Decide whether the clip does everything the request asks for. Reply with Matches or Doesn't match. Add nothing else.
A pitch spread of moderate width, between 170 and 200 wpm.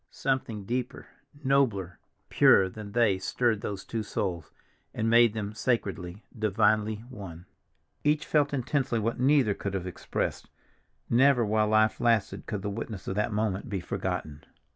Doesn't match